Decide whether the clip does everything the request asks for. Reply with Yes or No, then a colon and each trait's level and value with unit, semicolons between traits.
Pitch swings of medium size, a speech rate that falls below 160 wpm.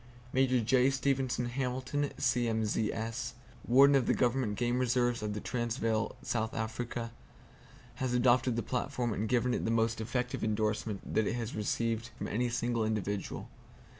No: narrow, 2.2 semitones; average, 150 wpm